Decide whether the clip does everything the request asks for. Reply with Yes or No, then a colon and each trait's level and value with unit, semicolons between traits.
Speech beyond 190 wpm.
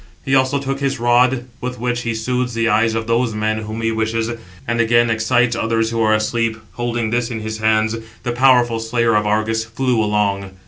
Yes: average, 200 wpm